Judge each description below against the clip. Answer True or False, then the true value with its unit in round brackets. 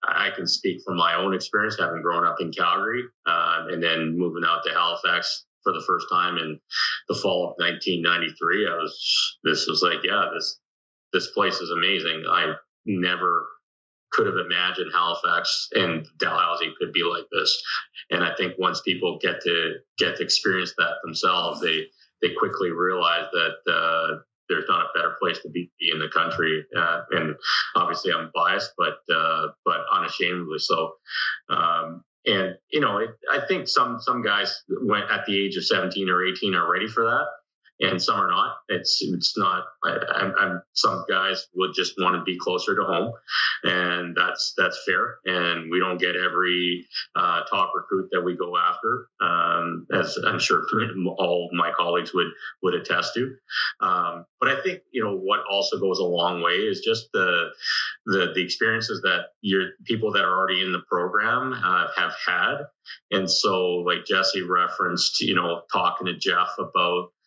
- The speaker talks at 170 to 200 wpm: True (180 wpm)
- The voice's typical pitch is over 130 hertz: False (125 Hz)